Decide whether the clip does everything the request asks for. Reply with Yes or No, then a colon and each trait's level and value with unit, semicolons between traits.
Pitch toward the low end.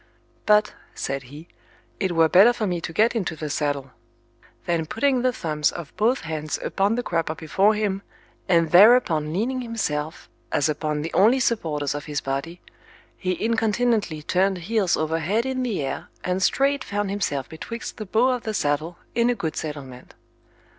No: medium, 180 Hz